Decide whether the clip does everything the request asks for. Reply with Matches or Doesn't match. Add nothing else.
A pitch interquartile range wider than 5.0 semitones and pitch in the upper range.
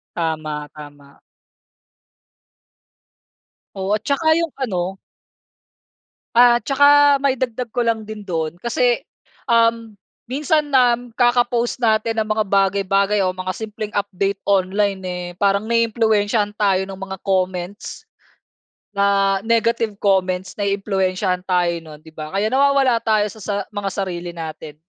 Doesn't match